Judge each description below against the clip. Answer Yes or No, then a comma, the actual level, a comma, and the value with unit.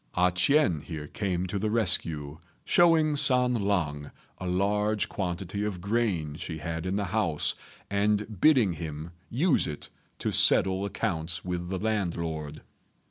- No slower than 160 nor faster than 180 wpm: No, average, 140 wpm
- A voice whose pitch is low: Yes, very low, 95 Hz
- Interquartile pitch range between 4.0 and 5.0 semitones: Yes, average, 4.3 semitones